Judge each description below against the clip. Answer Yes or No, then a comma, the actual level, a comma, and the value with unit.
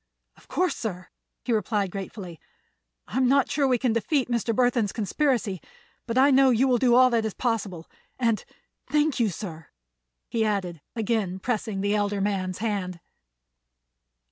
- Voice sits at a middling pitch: No, high, 220 Hz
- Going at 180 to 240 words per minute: No, average, 155 wpm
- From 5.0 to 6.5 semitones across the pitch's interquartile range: No, average, 4.2 semitones